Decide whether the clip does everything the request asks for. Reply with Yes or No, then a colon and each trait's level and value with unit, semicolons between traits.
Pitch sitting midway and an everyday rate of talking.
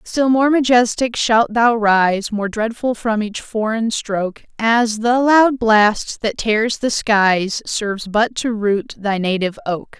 No: high, 220 Hz; average, 160 wpm